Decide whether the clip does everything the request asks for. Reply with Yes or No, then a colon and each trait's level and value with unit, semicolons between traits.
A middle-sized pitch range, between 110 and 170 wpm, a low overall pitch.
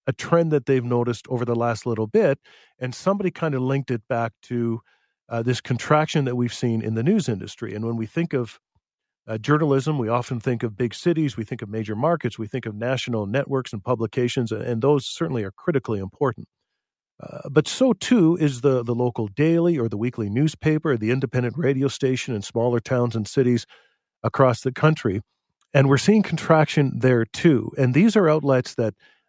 No: average, 4.3 semitones; average, 195 wpm; low, 130 Hz